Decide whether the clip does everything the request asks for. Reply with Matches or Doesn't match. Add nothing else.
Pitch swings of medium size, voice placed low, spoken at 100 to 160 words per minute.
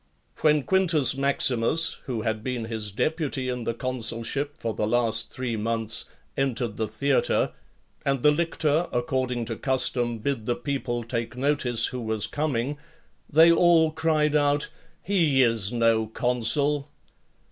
Matches